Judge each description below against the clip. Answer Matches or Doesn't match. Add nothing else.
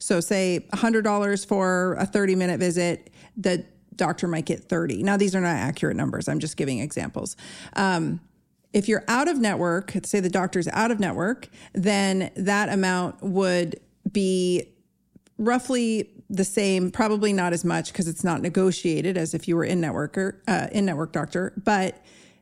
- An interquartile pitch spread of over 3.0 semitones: Doesn't match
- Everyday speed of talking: Matches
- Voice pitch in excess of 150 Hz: Matches